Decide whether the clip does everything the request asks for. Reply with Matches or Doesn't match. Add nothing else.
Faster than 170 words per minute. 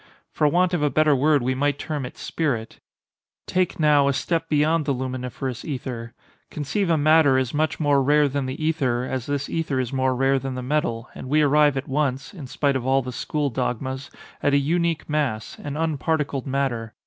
Matches